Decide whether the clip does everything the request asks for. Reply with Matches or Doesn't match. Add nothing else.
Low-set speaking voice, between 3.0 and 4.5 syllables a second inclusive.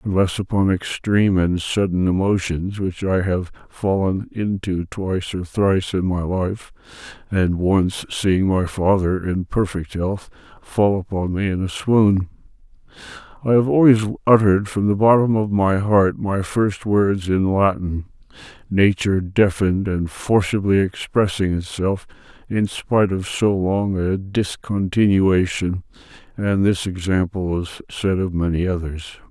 Matches